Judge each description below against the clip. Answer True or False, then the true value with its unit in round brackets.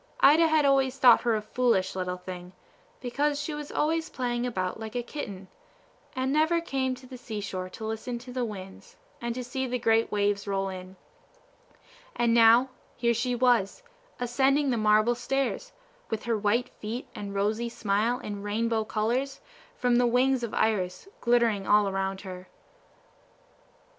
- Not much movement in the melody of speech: False (3.8 semitones)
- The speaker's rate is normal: True (165 wpm)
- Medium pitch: False (235 Hz)